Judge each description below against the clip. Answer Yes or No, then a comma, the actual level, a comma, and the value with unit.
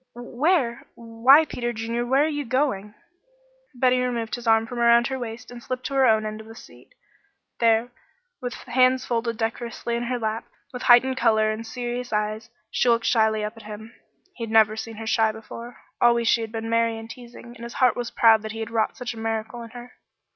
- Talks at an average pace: No, fast, 215 wpm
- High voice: Yes, high, 235 Hz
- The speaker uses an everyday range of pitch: No, narrow, 1.6 semitones